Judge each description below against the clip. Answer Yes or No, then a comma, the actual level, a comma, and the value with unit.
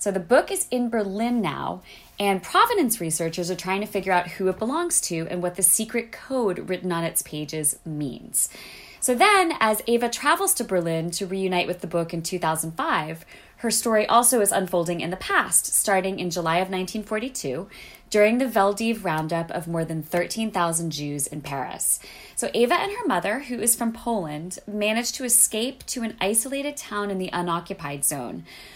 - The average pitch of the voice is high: Yes, high, 195 Hz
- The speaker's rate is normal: Yes, average, 180 wpm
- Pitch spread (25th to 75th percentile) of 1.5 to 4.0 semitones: No, wide, 5.4 semitones